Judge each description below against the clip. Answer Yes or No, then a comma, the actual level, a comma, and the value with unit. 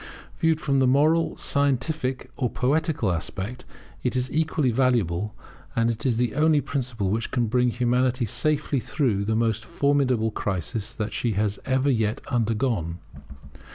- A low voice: Yes, low, 125 Hz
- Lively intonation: No, average, 3.8 semitones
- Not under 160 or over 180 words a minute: No, average, 150 wpm